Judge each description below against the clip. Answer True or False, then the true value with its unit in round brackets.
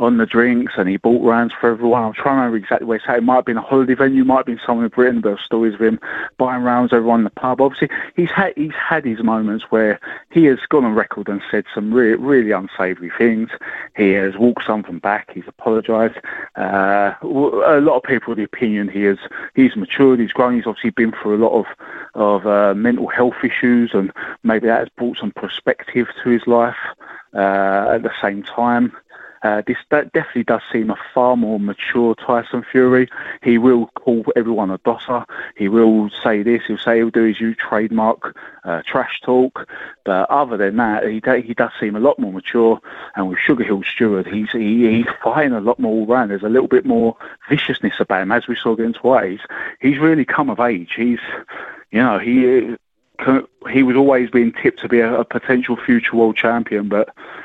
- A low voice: True (115 Hz)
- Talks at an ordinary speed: False (215 wpm)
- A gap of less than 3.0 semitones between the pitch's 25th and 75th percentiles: True (2.4 semitones)